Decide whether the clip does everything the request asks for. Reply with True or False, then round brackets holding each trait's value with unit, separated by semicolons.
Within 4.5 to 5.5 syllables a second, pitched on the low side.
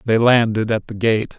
True (4.7 syllables/s; 110 Hz)